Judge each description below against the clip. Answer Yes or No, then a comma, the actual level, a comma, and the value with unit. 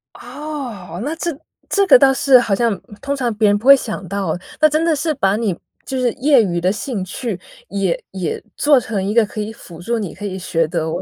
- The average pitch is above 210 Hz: Yes, high, 220 Hz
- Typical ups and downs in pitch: No, wide, 6.1 semitones